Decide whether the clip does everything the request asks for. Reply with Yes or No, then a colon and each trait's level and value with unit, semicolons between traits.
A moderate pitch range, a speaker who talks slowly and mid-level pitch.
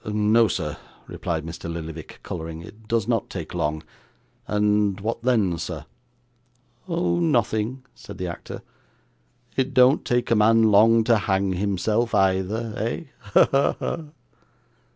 No: average, 4.1 semitones; slow, 130 wpm; low, 105 Hz